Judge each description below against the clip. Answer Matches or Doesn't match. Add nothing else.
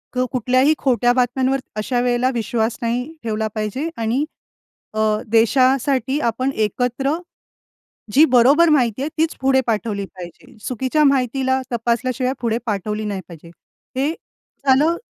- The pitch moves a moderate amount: Matches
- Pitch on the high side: Matches